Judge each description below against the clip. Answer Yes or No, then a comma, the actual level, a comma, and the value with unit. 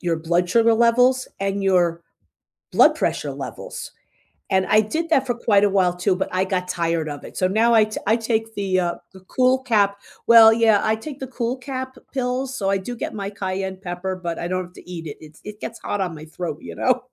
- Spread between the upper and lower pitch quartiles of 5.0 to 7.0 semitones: No, average, 4.4 semitones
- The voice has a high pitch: Yes, high, 200 Hz